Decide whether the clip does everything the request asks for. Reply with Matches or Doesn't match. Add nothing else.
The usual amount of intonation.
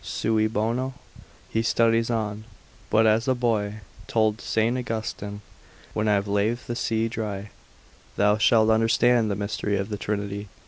Doesn't match